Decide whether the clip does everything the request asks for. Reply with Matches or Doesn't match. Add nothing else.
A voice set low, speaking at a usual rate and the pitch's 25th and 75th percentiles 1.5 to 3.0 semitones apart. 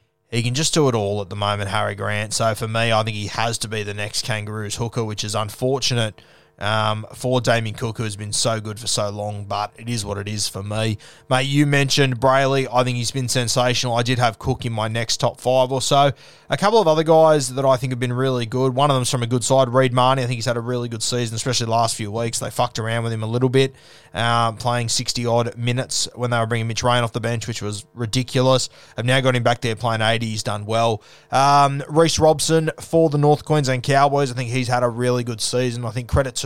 Doesn't match